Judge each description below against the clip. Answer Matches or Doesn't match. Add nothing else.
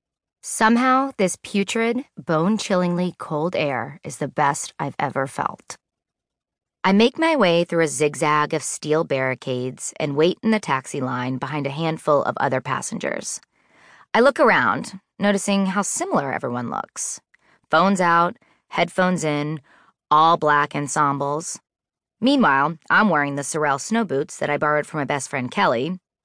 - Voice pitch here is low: Doesn't match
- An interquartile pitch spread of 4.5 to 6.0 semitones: Matches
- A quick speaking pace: Doesn't match